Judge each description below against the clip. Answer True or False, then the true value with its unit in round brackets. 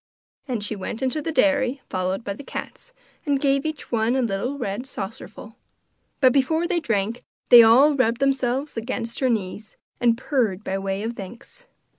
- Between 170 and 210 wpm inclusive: True (180 wpm)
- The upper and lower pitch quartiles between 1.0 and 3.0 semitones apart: False (4.3 semitones)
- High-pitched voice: True (245 Hz)